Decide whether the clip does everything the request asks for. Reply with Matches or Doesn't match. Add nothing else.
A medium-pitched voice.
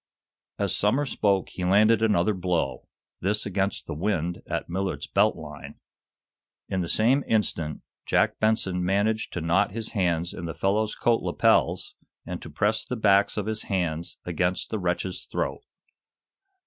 Doesn't match